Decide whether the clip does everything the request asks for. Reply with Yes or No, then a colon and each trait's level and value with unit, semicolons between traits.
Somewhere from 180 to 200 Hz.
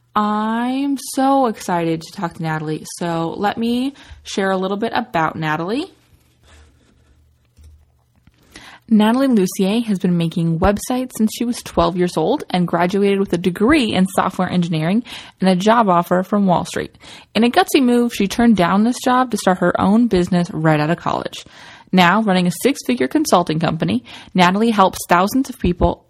Yes: high, 190 Hz